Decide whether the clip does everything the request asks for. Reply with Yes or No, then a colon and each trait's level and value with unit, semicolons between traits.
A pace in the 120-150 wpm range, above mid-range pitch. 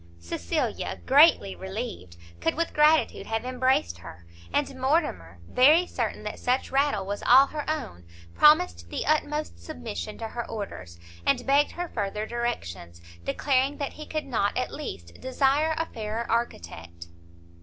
Yes: average, 145 wpm; high, 245 Hz